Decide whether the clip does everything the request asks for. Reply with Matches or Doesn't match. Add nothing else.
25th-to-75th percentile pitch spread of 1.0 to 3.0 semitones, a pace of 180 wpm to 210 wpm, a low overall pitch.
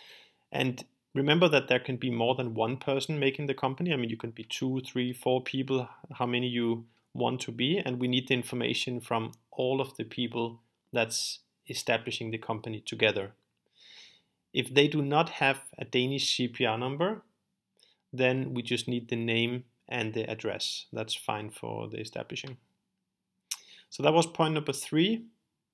Doesn't match